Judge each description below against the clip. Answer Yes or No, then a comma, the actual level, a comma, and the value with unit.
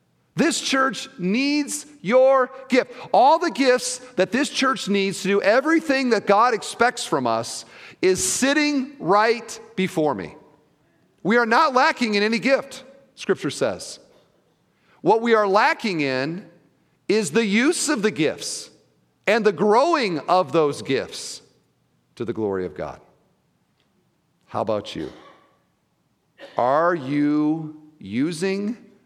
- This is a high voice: Yes, high, 215 Hz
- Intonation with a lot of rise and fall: Yes, wide, 7.1 semitones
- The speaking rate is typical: No, slow, 130 wpm